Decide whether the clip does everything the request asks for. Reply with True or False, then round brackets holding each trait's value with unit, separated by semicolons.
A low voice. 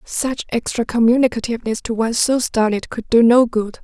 False (235 Hz)